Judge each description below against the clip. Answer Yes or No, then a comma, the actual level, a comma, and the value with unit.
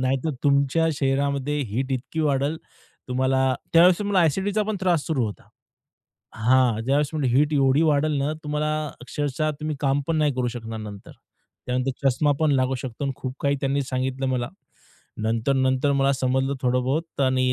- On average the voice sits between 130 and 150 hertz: Yes, low, 135 Hz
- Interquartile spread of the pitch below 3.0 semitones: Yes, narrow, 2.5 semitones